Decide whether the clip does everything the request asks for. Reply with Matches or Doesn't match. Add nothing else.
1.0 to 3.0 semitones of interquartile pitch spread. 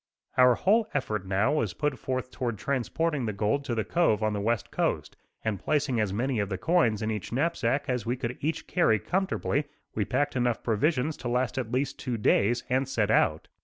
Doesn't match